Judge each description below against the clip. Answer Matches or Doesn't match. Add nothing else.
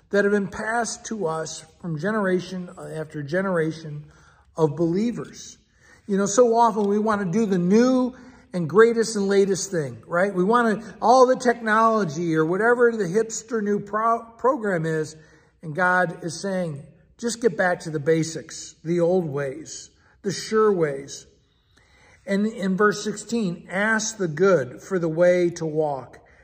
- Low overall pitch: Doesn't match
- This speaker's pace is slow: Doesn't match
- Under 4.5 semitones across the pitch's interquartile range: Doesn't match